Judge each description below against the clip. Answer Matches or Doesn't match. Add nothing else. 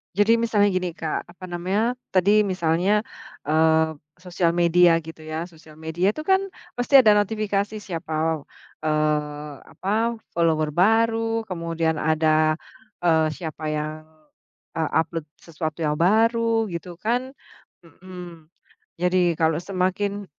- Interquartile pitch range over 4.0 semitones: Matches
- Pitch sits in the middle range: Matches